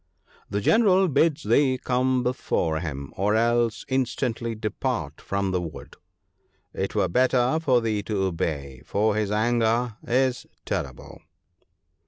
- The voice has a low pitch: Yes, low, 115 Hz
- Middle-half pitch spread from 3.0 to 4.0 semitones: No, average, 4.5 semitones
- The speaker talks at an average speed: No, slow, 130 wpm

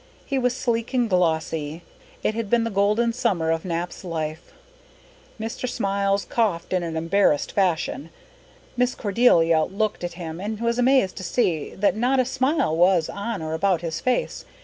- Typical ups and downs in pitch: No, wide, 5.8 semitones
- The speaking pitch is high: Yes, high, 195 Hz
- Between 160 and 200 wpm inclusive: Yes, average, 170 wpm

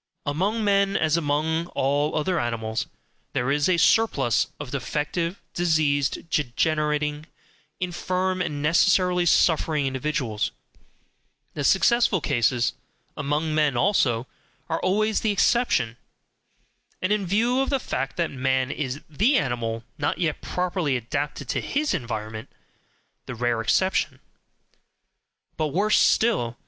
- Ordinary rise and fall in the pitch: No, wide, 5.7 semitones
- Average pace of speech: No, slow, 120 wpm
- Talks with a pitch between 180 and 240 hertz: No, medium, 150 Hz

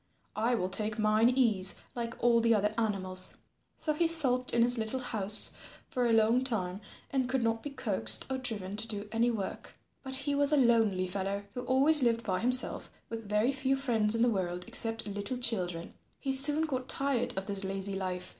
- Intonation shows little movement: No, average, 4.2 semitones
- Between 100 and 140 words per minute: No, average, 200 wpm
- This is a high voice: Yes, high, 230 Hz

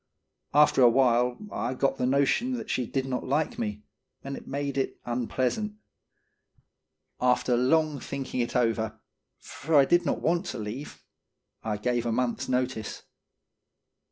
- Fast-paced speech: No, average, 150 wpm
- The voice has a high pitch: No, low, 130 Hz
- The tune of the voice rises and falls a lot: No, average, 2.7 semitones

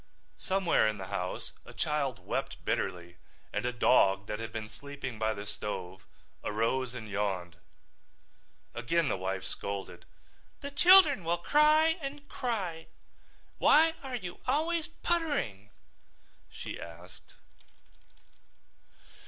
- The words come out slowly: Yes, slow, 120 wpm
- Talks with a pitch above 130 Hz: No, low, 125 Hz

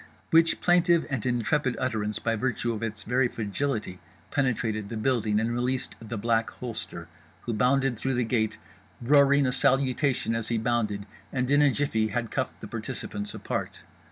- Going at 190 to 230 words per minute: No, average, 170 wpm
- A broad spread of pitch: No, average, 3.2 semitones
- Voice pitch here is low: Yes, low, 120 Hz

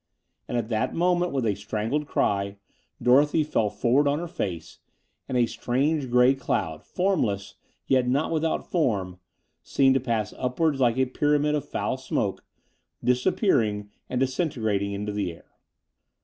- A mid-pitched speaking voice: No, low, 125 Hz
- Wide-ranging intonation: Yes, wide, 5.9 semitones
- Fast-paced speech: No, average, 150 wpm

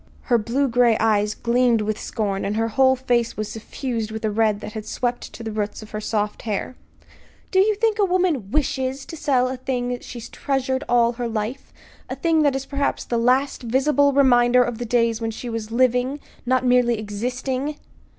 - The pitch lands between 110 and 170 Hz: No, high, 245 Hz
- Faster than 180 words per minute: Yes, average, 200 wpm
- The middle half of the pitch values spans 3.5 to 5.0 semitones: No, average, 3.0 semitones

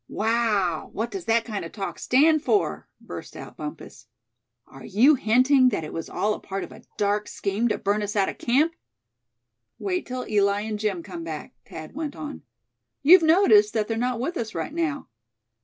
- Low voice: No, high, 225 Hz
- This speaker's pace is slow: No, average, 190 wpm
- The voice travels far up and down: Yes, wide, 5.8 semitones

